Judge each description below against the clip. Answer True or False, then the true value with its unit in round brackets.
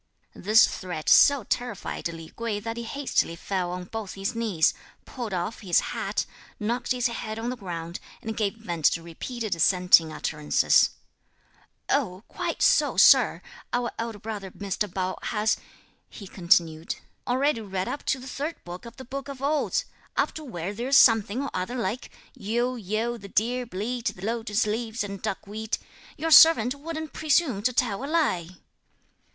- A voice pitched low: False (220 Hz)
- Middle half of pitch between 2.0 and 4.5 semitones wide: False (4.9 semitones)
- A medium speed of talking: True (165 wpm)